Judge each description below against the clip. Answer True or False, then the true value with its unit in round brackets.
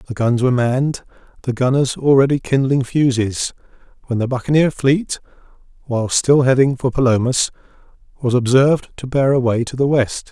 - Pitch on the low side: True (130 Hz)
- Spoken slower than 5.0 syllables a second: False (5.2 syllables/s)